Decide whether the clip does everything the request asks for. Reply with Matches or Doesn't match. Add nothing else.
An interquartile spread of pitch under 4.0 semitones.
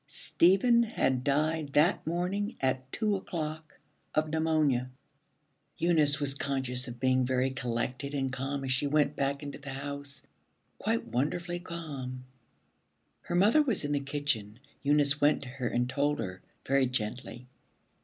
Matches